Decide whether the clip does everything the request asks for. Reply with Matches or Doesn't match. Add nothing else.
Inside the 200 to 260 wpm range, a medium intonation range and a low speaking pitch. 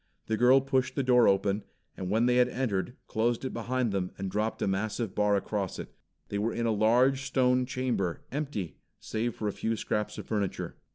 Matches